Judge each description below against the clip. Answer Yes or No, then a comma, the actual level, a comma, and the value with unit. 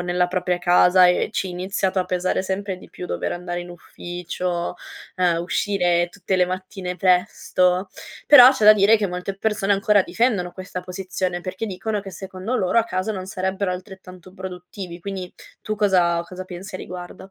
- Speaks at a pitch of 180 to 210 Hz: Yes, medium, 185 Hz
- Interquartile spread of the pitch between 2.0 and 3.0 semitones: No, narrow, 1.6 semitones